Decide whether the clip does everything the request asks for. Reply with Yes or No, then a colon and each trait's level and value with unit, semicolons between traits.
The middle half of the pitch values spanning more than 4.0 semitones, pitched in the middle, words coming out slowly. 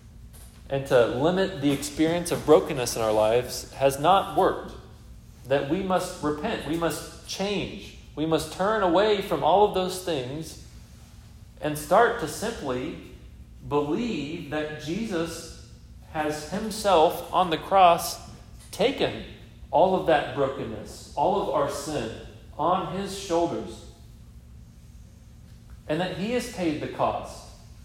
Yes: average, 4.6 semitones; medium, 155 Hz; slow, 130 wpm